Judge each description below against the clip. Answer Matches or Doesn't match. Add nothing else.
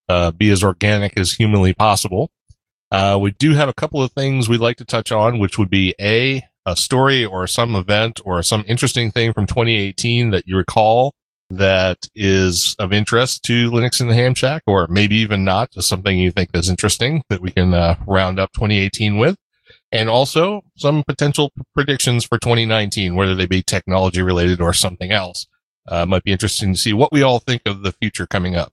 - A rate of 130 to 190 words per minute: Doesn't match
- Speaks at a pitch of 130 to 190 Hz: Doesn't match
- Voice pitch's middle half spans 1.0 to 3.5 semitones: Doesn't match